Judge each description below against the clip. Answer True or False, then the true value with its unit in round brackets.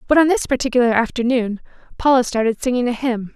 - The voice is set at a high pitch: True (245 Hz)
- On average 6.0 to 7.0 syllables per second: True (6.3 syllables/s)